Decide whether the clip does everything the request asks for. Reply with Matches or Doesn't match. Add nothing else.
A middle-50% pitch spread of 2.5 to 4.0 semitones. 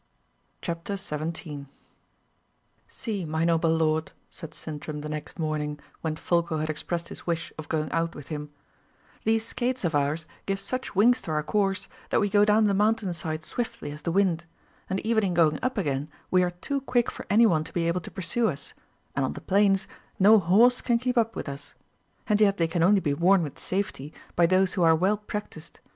Doesn't match